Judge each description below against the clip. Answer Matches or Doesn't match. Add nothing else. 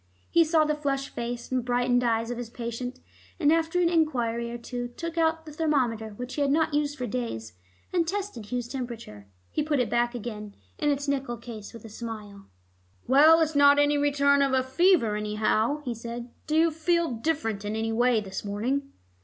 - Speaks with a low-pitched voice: Doesn't match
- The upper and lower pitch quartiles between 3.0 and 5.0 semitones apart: Matches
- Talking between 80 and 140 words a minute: Doesn't match